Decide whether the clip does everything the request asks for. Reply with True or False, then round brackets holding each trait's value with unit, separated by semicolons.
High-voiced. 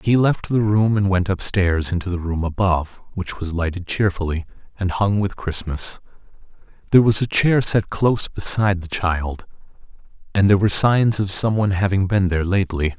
False (95 Hz)